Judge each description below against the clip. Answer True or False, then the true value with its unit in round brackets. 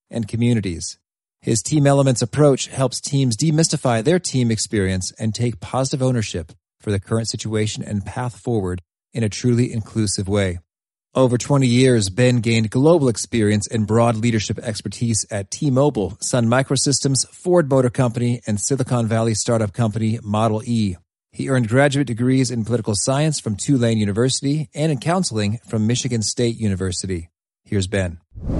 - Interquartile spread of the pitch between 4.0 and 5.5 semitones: False (3.5 semitones)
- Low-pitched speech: True (115 Hz)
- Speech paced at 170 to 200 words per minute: False (155 wpm)